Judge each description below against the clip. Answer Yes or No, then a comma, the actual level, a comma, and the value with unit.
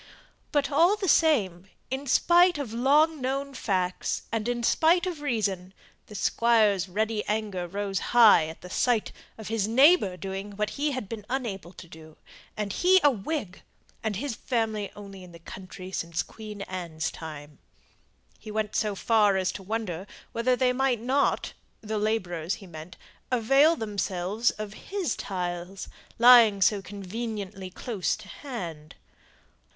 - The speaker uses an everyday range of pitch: Yes, average, 5.0 semitones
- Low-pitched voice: No, high, 210 Hz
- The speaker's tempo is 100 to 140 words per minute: No, average, 155 wpm